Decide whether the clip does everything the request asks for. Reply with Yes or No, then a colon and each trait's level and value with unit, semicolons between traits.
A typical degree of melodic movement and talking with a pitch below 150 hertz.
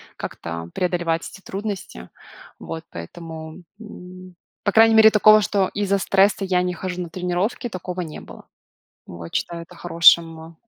No: average, 3.2 semitones; medium, 180 Hz